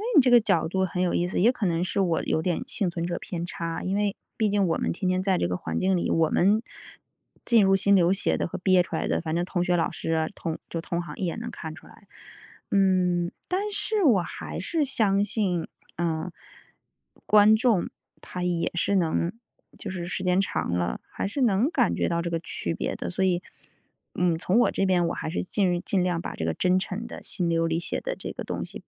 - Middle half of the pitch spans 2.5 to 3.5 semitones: Yes, average, 2.9 semitones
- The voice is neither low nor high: Yes, medium, 180 Hz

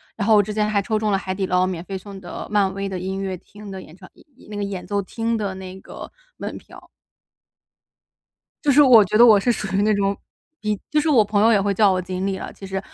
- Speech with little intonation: Yes, narrow, 1.9 semitones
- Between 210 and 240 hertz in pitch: No, high, 200 Hz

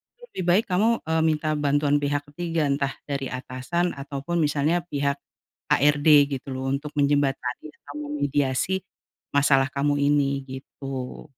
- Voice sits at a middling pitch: Yes, medium, 145 Hz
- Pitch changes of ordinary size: No, narrow, 2.0 semitones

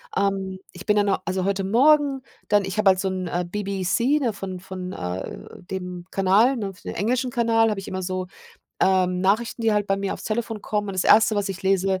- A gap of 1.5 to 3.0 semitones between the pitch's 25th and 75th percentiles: Yes, narrow, 2.5 semitones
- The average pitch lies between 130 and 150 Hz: No, high, 195 Hz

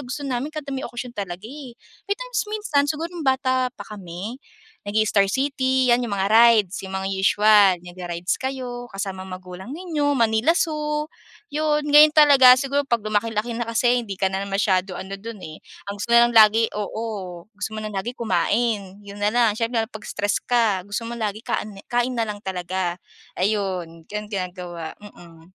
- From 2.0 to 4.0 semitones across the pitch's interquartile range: No, average, 5.0 semitones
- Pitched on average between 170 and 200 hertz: No, high, 220 Hz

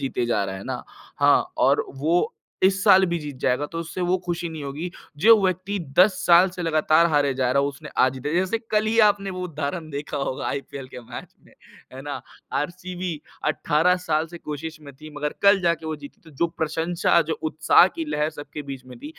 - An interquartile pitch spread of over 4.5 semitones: No, average, 3.8 semitones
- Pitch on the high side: No, medium, 160 Hz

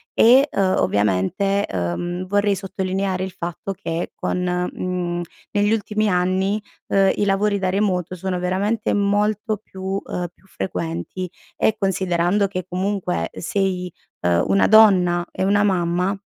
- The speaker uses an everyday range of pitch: No, narrow, 2.2 semitones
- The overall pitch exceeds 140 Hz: Yes, high, 190 Hz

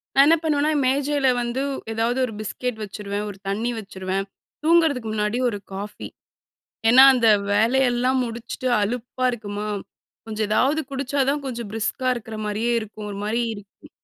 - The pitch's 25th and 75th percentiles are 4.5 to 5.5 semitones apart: No, average, 3.8 semitones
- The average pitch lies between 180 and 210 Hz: No, high, 235 Hz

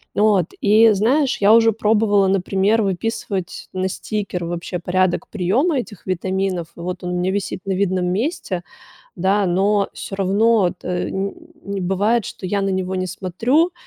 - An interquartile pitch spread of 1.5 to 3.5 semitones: Yes, average, 2.7 semitones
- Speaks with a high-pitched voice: Yes, high, 195 Hz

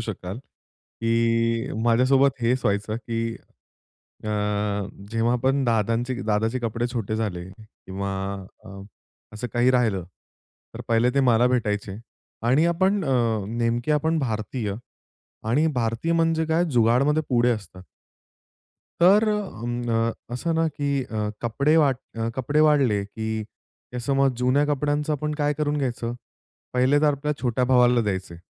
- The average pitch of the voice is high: No, low, 120 Hz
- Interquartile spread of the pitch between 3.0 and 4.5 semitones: Yes, average, 3.7 semitones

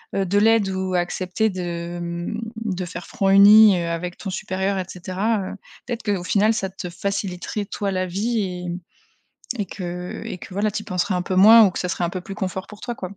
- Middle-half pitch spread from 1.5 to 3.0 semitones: Yes, narrow, 2.5 semitones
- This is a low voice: No, high, 190 Hz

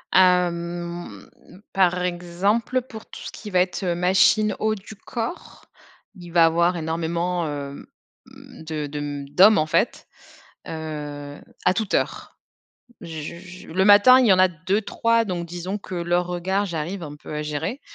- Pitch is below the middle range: No, medium, 175 Hz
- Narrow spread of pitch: No, average, 3.2 semitones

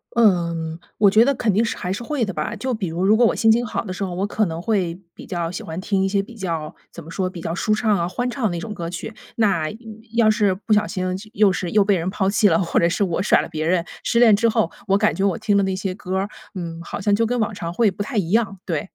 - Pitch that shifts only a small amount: No, average, 3.6 semitones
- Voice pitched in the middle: No, high, 195 Hz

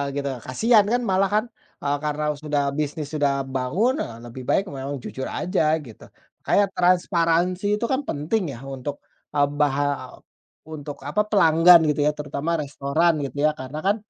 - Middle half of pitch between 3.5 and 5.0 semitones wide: Yes, average, 4.1 semitones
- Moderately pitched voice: Yes, medium, 150 Hz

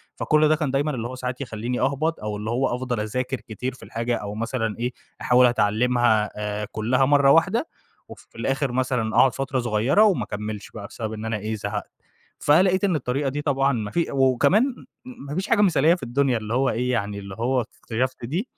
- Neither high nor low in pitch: No, low, 125 Hz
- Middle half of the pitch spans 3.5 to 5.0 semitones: Yes, average, 4.0 semitones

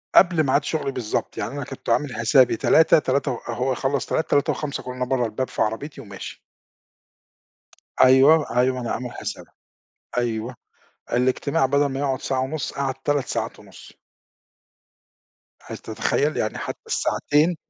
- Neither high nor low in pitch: No, low, 130 Hz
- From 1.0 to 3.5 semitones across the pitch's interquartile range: Yes, narrow, 2.6 semitones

